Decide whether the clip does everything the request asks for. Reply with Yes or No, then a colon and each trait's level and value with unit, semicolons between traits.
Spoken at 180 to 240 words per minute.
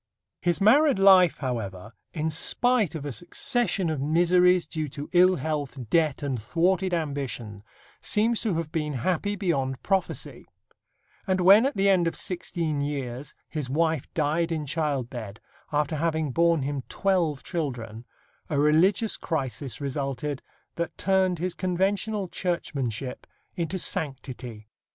No: slow, 135 wpm